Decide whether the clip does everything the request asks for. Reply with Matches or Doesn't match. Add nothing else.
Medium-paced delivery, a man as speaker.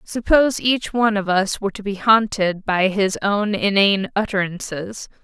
Doesn't match